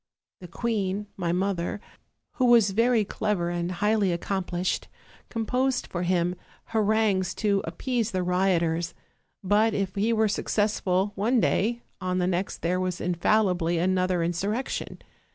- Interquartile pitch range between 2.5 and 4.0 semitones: Yes, average, 3.4 semitones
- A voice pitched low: No, high, 195 Hz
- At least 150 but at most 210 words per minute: No, average, 140 wpm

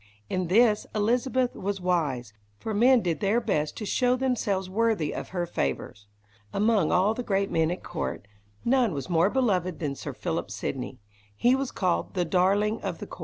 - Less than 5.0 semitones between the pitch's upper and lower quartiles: No, wide, 5.6 semitones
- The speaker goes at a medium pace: Yes, average, 180 wpm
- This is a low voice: No, high, 195 Hz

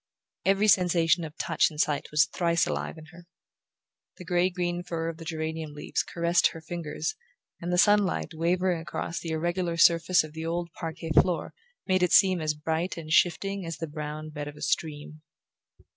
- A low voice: No, medium, 165 Hz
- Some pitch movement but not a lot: No, narrow, 1.9 semitones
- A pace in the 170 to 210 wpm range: Yes, average, 185 wpm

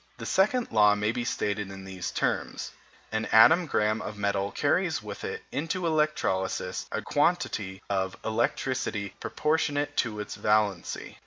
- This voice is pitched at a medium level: No, low, 110 Hz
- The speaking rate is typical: Yes, average, 145 wpm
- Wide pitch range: Yes, wide, 6.3 semitones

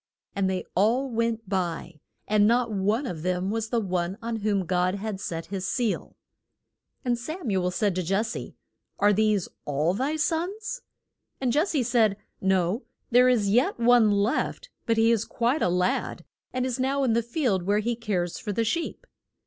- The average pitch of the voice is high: Yes, high, 215 Hz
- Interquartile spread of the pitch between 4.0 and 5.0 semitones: Yes, average, 4.3 semitones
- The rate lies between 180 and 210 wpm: Yes, average, 190 wpm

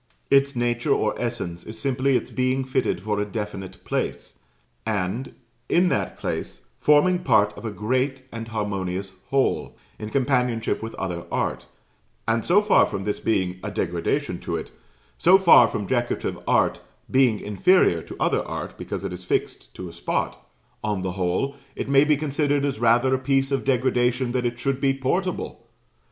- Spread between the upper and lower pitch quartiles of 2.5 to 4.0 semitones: No, average, 4.7 semitones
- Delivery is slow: No, average, 170 wpm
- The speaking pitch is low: Yes, low, 120 Hz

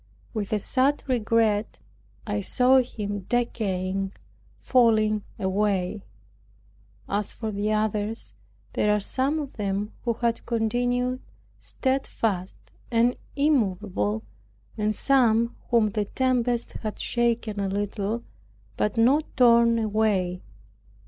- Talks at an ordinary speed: No, slow, 110 wpm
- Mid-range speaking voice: No, high, 220 Hz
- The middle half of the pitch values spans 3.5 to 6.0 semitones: No, average, 2.9 semitones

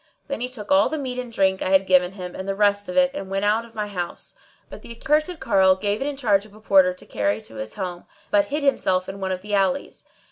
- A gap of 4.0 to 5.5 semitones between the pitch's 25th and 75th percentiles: Yes, average, 4.6 semitones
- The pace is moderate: No, fast, 275 wpm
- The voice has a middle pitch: No, high, 200 Hz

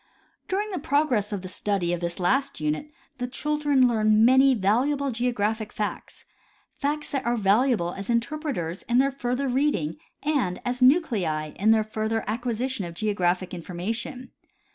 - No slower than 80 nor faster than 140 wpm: No, average, 155 wpm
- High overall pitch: Yes, high, 230 Hz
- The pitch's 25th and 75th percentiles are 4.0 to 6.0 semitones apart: Yes, wide, 5.5 semitones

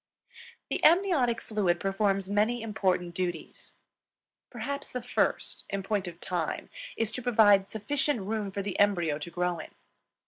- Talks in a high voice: Yes, high, 205 Hz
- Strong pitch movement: No, average, 3.9 semitones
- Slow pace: No, average, 145 wpm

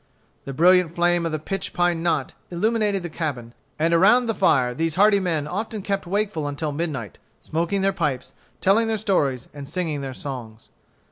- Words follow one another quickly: No, average, 180 wpm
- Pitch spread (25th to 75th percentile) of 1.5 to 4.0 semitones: No, average, 5.1 semitones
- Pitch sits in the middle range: Yes, medium, 170 Hz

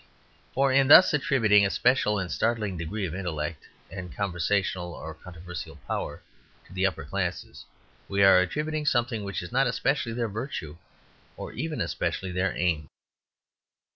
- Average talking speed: Yes, average, 150 wpm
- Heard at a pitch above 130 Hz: No, low, 100 Hz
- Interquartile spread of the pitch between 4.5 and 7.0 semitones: Yes, wide, 5.5 semitones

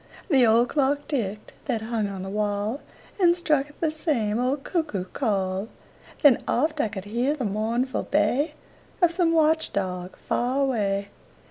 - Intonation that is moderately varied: No, wide, 6.1 semitones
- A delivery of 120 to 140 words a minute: No, average, 160 wpm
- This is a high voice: Yes, high, 240 Hz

